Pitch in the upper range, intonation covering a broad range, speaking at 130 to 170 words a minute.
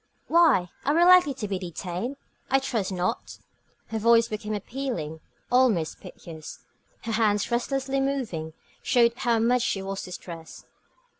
Yes: high, 225 Hz; wide, 6.0 semitones; average, 140 wpm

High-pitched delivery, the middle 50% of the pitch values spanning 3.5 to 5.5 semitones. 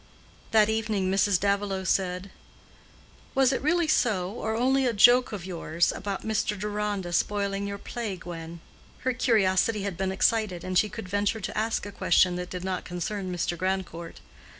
No: high, 200 Hz; average, 3.0 semitones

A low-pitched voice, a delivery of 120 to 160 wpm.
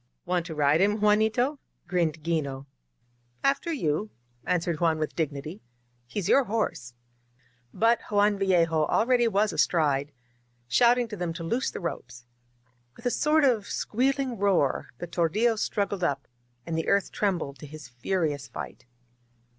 No: medium, 180 Hz; average, 150 wpm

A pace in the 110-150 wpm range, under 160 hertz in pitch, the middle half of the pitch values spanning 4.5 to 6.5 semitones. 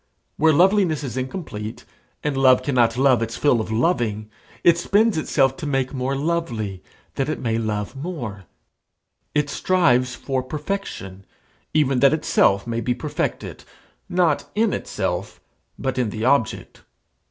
Yes: average, 140 wpm; low, 135 Hz; average, 5.3 semitones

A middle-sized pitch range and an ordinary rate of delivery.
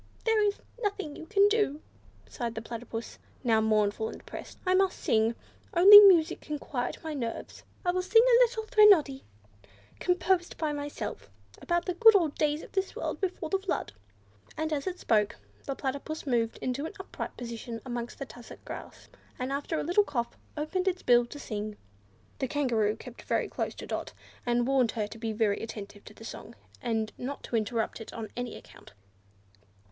No: wide, 7.8 semitones; average, 185 wpm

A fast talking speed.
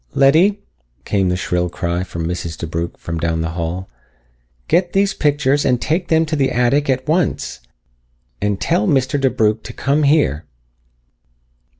No: average, 155 wpm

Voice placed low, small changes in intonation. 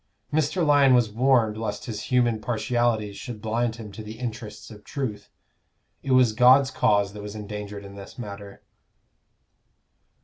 No: low, 110 Hz; average, 3.3 semitones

